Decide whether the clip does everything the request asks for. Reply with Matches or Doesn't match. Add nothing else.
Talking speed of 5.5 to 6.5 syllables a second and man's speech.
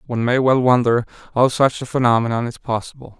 Matches